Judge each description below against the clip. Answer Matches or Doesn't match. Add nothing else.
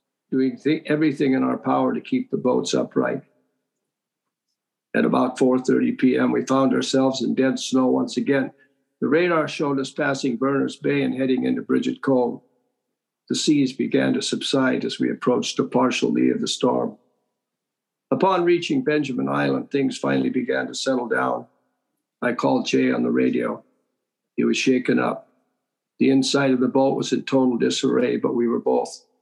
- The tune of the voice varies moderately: Doesn't match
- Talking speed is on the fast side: Doesn't match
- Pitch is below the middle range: Matches